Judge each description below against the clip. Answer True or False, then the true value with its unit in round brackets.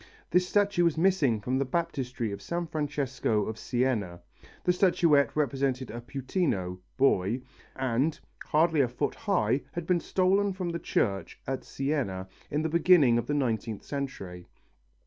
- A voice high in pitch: False (135 Hz)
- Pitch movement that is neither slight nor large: False (6.3 semitones)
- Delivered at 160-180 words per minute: False (150 wpm)